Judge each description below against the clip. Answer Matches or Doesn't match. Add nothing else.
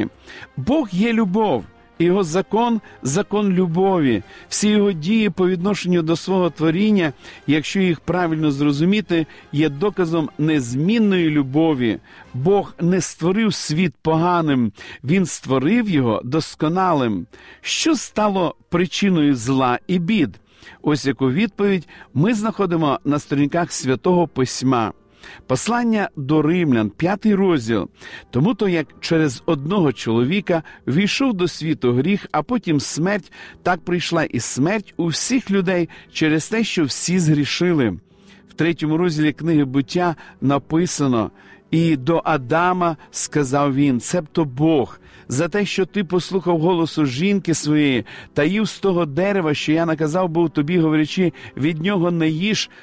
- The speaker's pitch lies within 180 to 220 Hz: Doesn't match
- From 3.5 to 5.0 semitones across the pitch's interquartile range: Matches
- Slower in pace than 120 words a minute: Doesn't match